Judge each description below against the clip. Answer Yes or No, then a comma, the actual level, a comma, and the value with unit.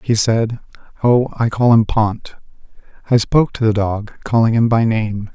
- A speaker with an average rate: Yes, average, 180 wpm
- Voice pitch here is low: Yes, low, 110 Hz